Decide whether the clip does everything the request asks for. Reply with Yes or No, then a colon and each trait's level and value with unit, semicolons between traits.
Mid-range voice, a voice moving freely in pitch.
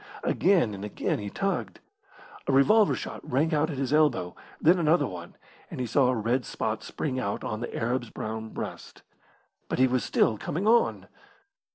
No: low, 130 Hz; wide, 5.9 semitones